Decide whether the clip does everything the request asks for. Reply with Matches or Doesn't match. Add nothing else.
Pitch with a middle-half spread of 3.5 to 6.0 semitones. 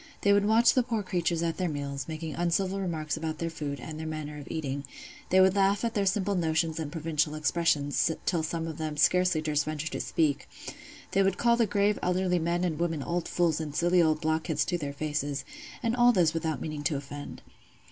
Doesn't match